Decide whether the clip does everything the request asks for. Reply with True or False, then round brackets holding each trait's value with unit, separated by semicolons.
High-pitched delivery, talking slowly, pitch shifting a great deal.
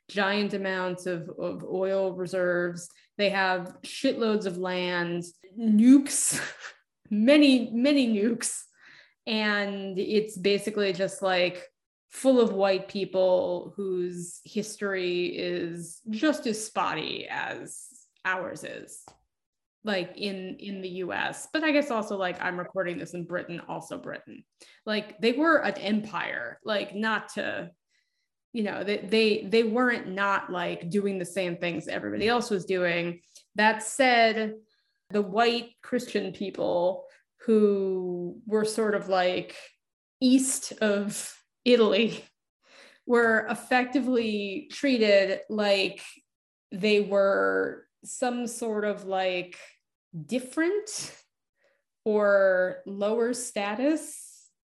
False (205 Hz; 110 wpm; 3.9 semitones)